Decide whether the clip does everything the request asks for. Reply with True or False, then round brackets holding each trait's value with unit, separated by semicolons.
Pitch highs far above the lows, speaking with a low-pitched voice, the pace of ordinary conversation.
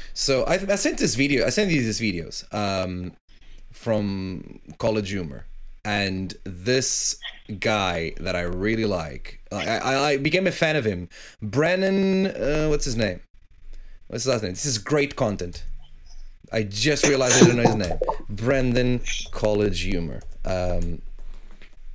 True (7.0 semitones; 105 Hz; 150 wpm)